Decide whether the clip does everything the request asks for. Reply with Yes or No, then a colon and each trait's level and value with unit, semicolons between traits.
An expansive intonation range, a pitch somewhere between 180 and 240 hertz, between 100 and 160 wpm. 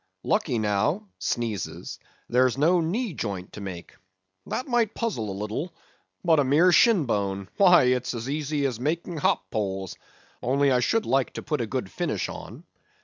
No: wide, 8.1 semitones; low, 135 Hz; average, 155 wpm